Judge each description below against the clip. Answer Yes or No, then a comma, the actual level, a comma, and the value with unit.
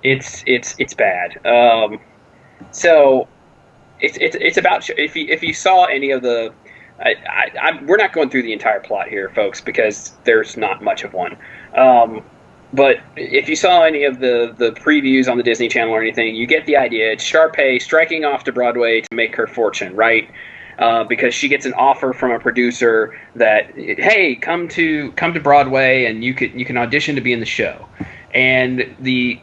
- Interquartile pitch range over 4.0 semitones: Yes, average, 4.5 semitones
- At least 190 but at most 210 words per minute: Yes, average, 195 wpm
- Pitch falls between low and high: No, low, 130 Hz